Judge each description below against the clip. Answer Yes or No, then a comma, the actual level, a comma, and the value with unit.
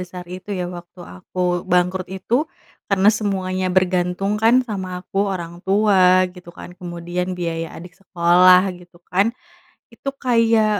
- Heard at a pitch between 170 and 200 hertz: Yes, medium, 185 Hz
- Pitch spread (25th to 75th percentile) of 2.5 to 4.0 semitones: No, narrow, 1.7 semitones